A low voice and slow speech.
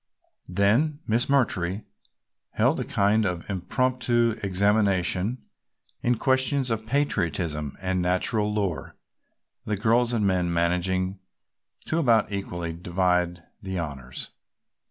Yes: low, 100 Hz; slow, 110 wpm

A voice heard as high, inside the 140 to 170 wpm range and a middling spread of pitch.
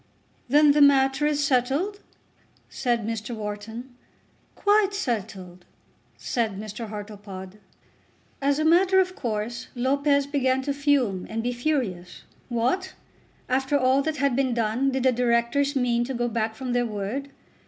Yes: very high, 250 Hz; average, 145 wpm; average, 4.1 semitones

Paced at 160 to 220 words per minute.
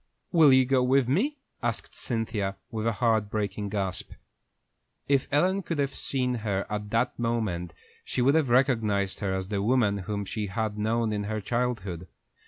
Yes: average, 175 wpm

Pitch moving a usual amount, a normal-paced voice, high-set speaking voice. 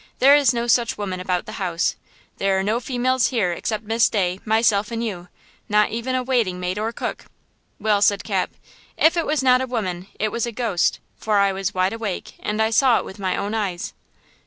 No: average, 3.6 semitones; fast, 210 wpm; high, 215 Hz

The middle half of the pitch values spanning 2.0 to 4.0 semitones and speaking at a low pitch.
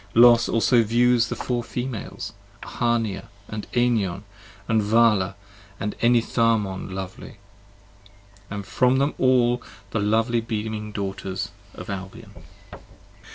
Yes: average, 2.8 semitones; low, 115 Hz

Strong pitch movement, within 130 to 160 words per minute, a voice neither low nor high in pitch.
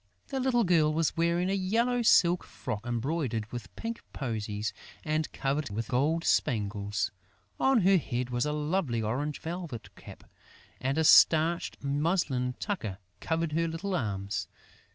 Yes: wide, 6.4 semitones; average, 145 wpm; medium, 150 Hz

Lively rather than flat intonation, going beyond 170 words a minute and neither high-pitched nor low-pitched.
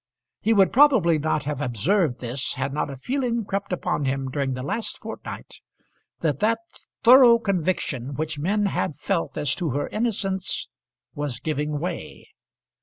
No: wide, 6.5 semitones; average, 155 wpm; medium, 160 Hz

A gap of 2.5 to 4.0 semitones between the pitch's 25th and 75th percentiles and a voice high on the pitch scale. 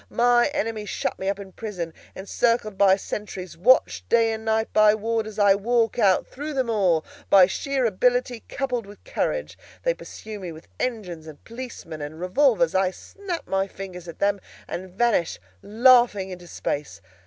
No: average, 4.5 semitones; high, 210 Hz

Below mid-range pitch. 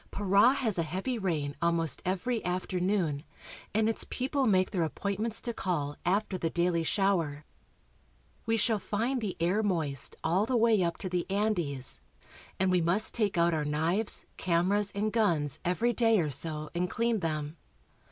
No: medium, 185 Hz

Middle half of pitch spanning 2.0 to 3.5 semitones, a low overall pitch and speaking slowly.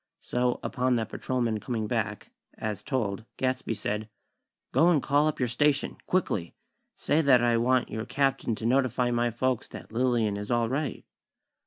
No: average, 2.8 semitones; low, 120 Hz; average, 165 wpm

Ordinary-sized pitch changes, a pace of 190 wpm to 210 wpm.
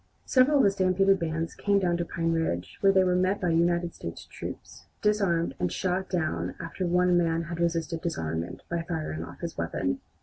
No: narrow, 2.2 semitones; average, 195 wpm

